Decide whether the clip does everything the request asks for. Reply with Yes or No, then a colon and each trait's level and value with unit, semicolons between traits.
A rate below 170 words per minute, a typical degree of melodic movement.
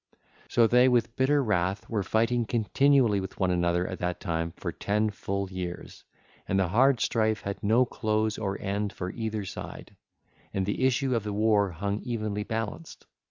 No: average, 175 wpm; average, 3.0 semitones